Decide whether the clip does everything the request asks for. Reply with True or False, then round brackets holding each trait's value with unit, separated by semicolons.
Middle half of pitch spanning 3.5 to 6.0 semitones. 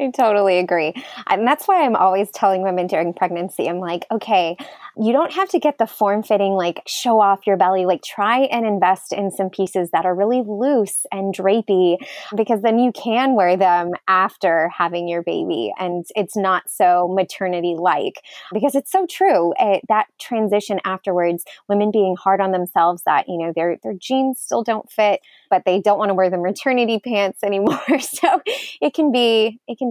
True (4.2 semitones)